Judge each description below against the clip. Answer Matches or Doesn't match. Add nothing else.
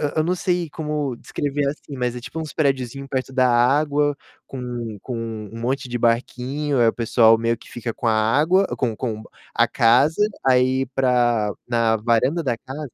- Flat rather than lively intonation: Doesn't match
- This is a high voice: Doesn't match